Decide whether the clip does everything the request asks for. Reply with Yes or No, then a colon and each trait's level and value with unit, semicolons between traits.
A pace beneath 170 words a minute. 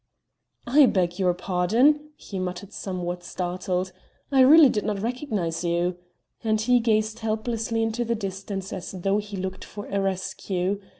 Yes: average, 155 wpm